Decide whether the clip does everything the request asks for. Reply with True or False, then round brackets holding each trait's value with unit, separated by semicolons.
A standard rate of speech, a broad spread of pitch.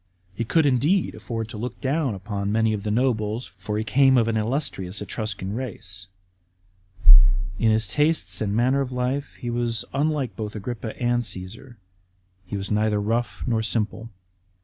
False (165 wpm; 3.2 semitones)